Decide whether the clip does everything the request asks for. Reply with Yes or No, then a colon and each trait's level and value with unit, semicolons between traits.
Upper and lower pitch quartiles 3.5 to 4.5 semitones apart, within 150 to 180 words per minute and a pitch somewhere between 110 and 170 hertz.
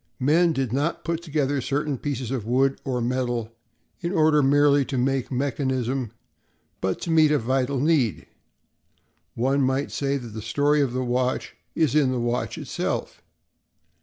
No: narrow, 2.6 semitones; average, 165 wpm; low, 135 Hz